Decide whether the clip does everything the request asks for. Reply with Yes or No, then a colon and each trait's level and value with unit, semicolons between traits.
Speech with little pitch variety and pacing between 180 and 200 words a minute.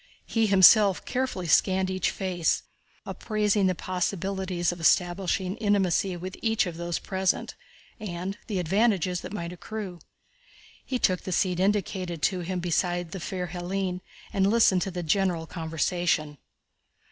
No: narrow, 2.1 semitones; average, 140 wpm